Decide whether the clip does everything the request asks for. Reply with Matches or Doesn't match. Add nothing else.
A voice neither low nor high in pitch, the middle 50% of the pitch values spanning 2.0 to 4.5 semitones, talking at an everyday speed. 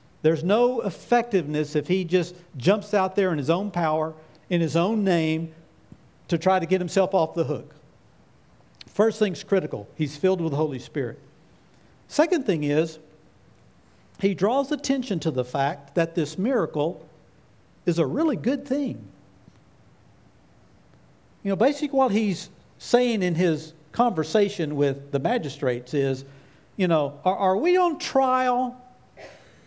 Doesn't match